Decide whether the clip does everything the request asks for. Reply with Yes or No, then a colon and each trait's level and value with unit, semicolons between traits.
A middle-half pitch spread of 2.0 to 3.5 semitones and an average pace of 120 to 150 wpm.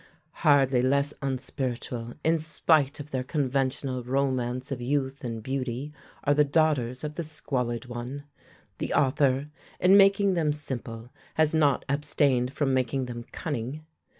Yes: average, 2.8 semitones; average, 140 wpm